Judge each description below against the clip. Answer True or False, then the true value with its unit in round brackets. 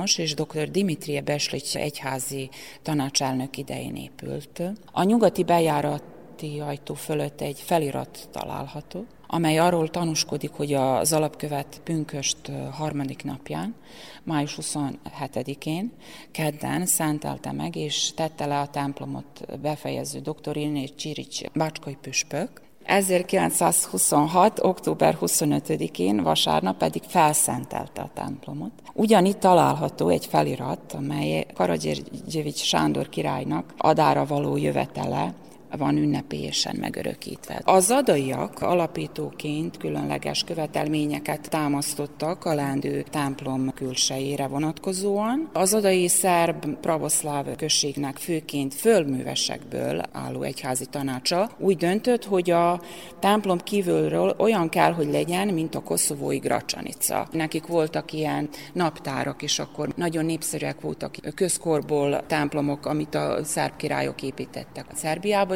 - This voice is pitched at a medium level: True (150 Hz)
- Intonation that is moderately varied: True (3.5 semitones)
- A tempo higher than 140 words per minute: False (105 wpm)